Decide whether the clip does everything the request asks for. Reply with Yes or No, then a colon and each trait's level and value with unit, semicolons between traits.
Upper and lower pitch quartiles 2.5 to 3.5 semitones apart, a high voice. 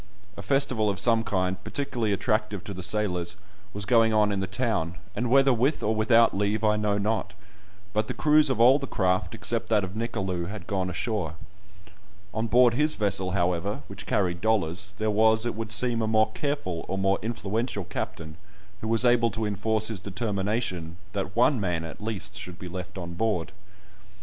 No: average, 3.2 semitones; low, 105 Hz